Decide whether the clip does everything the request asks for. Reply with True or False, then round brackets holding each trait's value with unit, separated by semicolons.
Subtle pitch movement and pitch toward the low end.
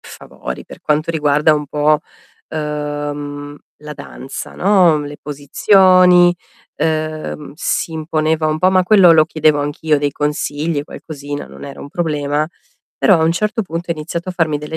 False (2.3 semitones; 155 Hz)